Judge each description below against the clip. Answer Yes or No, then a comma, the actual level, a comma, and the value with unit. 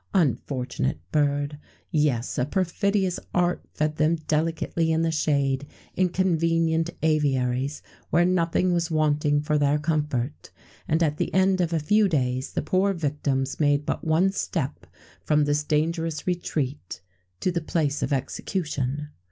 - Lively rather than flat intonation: No, average, 2.7 semitones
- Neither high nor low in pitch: Yes, medium, 155 Hz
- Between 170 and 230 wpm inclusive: No, average, 145 wpm